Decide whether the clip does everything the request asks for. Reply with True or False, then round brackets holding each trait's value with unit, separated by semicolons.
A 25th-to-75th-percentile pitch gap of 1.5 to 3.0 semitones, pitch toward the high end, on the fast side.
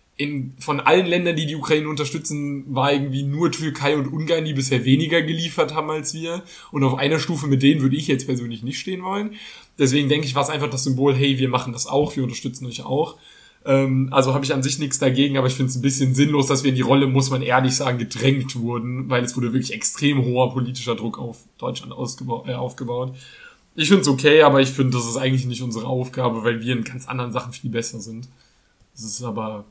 False (2.5 semitones; 135 Hz; 230 wpm)